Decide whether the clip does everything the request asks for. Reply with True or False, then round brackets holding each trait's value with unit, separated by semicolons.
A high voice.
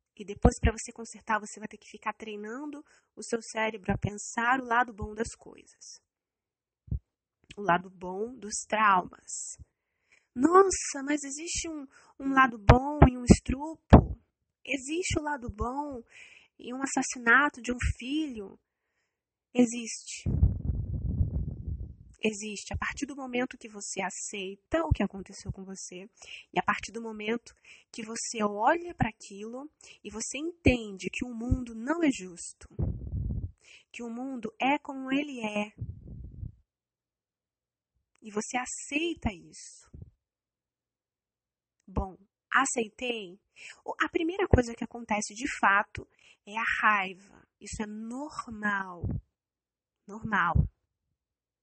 True (235 Hz)